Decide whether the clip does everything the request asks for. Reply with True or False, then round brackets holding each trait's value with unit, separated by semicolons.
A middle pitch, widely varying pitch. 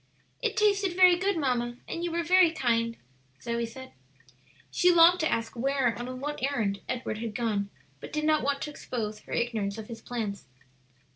False (255 Hz; 6.3 semitones)